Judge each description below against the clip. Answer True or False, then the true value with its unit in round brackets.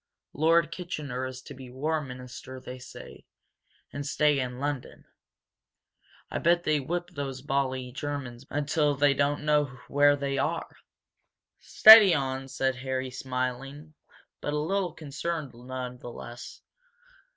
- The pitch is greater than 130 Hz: True (140 Hz)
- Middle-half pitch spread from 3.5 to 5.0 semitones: False (2.7 semitones)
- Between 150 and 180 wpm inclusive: False (140 wpm)